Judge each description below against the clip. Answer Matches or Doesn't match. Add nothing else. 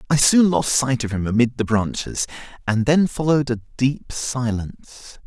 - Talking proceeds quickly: Doesn't match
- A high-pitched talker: Doesn't match